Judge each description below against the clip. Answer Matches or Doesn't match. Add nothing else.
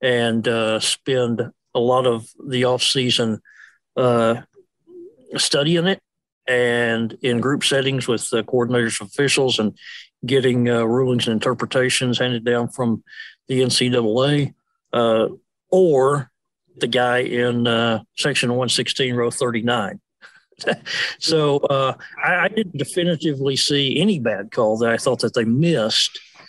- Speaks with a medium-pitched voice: Doesn't match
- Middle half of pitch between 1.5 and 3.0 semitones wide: Matches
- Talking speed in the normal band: Doesn't match